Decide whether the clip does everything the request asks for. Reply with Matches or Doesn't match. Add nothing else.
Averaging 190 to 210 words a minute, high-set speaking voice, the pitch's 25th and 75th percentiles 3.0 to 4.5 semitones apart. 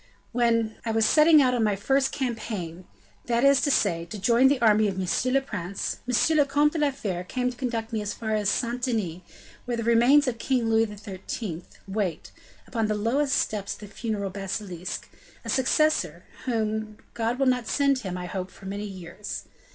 Matches